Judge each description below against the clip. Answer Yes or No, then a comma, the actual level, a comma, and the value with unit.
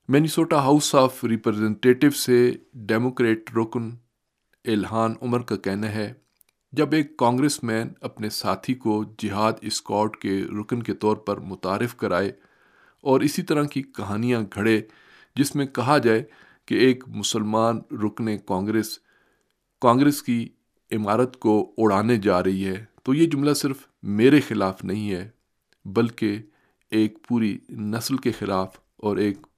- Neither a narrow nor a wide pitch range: Yes, average, 3.3 semitones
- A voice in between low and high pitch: No, low, 115 Hz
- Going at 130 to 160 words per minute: Yes, average, 135 wpm